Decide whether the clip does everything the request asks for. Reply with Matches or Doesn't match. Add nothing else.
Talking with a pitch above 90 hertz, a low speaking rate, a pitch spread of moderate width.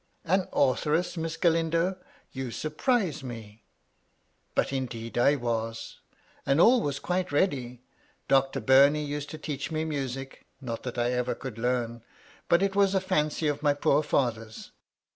Doesn't match